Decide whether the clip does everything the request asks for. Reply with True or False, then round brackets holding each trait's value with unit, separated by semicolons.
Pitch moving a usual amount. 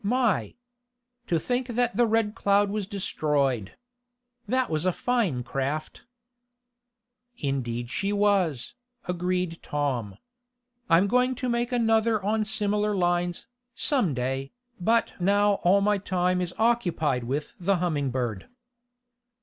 False (6.8 semitones)